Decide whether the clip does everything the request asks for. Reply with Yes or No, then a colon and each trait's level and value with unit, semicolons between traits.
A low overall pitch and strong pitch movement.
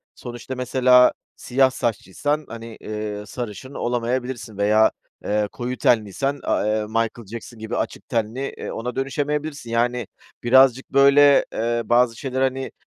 No: low, 120 Hz; average, 2.9 semitones